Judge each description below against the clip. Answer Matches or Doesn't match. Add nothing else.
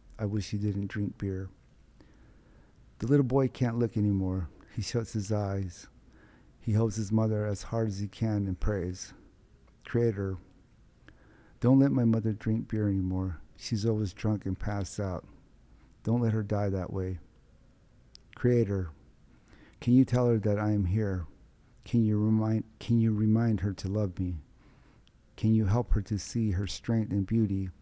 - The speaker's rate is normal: Matches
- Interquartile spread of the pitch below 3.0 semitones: Matches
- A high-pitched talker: Doesn't match